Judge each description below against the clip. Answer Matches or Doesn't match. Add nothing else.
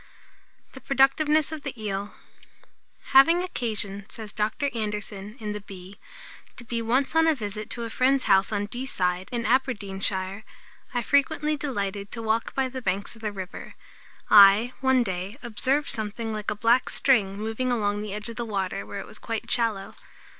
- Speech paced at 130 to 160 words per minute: Doesn't match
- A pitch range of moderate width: Matches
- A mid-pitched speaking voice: Doesn't match